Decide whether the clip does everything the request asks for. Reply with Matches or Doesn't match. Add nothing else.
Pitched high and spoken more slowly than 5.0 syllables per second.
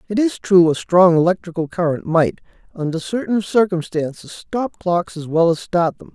Doesn't match